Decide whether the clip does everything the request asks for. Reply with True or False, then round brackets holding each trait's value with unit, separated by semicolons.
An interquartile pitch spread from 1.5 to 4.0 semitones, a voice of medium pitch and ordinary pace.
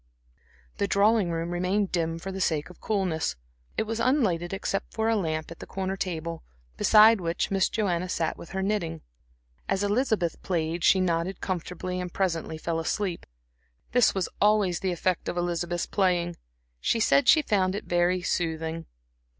True (3.1 semitones; 180 Hz; 165 wpm)